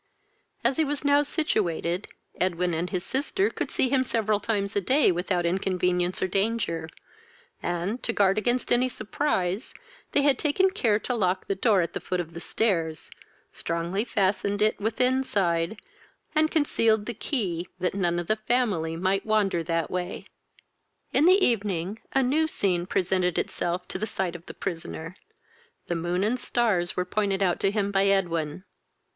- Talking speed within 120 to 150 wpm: No, average, 170 wpm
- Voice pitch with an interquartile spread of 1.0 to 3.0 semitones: No, average, 4.8 semitones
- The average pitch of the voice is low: No, high, 195 Hz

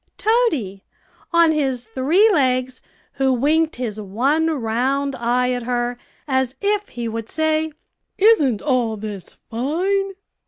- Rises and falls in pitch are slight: No, average, 4.9 semitones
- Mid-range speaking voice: No, very high, 260 Hz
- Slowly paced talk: Yes, slow, 125 wpm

